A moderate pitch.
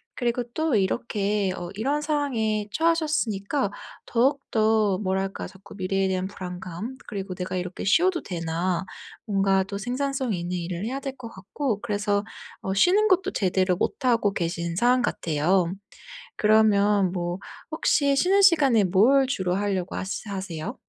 No: high, 205 Hz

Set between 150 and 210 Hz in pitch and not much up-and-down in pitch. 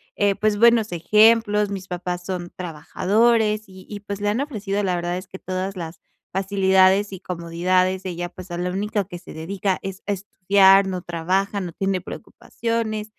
Yes: high, 190 Hz; narrow, 2.3 semitones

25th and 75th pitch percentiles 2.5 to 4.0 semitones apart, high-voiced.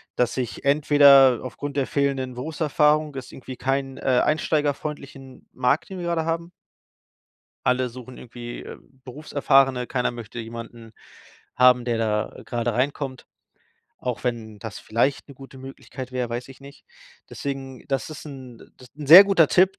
No: average, 2.8 semitones; low, 135 Hz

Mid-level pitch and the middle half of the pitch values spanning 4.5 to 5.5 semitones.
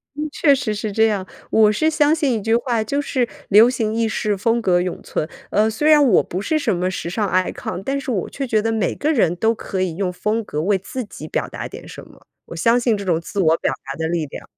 No: high, 215 Hz; average, 4.8 semitones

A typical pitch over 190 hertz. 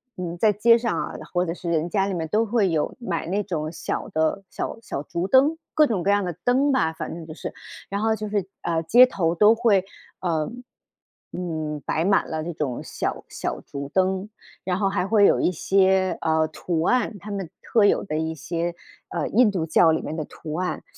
No: medium, 185 Hz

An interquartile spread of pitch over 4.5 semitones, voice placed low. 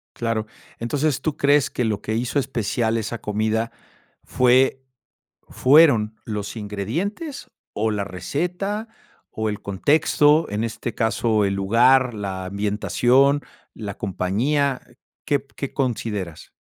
Yes: average, 5.1 semitones; low, 115 Hz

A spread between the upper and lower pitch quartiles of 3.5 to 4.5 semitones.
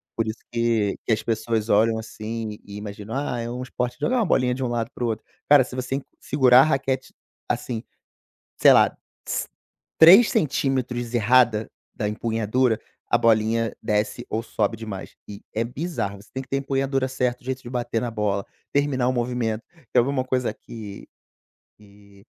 No: average, 2.9 semitones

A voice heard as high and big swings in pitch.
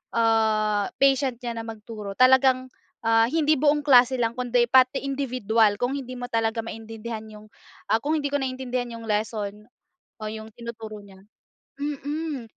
No: high, 235 Hz; average, 3.1 semitones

